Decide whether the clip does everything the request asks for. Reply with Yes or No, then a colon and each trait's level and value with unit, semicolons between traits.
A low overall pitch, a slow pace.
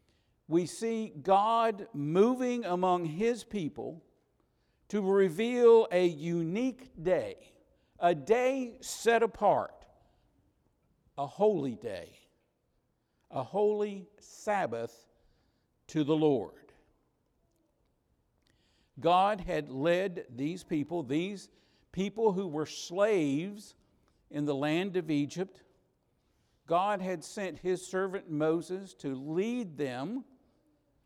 No: medium, 185 Hz; slow, 95 wpm